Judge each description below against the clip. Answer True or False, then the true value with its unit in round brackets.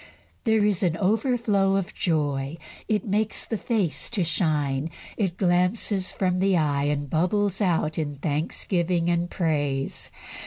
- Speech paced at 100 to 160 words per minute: True (140 wpm)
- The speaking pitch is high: False (175 Hz)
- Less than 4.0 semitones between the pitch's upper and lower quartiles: False (4.6 semitones)